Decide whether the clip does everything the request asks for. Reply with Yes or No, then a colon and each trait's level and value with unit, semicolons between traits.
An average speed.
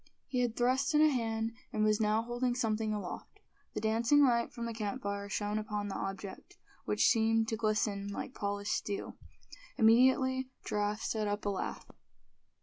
Yes: average, 165 wpm